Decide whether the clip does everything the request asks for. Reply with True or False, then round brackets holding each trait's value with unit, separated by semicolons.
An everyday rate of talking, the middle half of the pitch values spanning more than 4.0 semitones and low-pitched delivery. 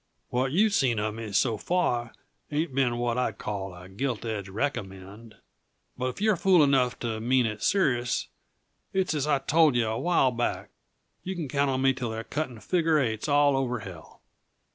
True (185 wpm; 4.6 semitones; 125 Hz)